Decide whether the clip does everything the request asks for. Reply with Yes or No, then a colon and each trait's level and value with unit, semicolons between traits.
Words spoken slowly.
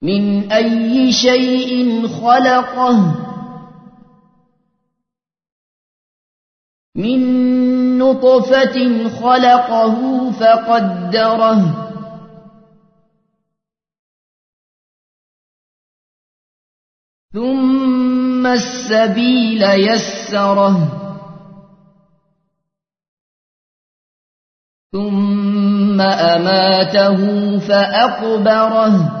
Yes: slow, 30 wpm